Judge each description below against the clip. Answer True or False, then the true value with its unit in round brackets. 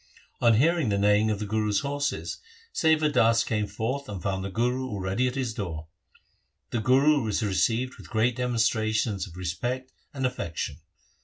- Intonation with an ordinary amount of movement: True (3.9 semitones)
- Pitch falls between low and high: False (115 Hz)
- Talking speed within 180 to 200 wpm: False (165 wpm)